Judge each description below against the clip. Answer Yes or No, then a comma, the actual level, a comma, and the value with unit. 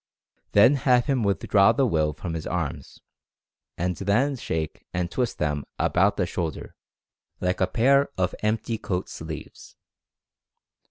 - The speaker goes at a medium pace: Yes, average, 150 wpm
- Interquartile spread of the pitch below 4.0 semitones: No, wide, 5.6 semitones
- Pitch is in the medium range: No, low, 100 Hz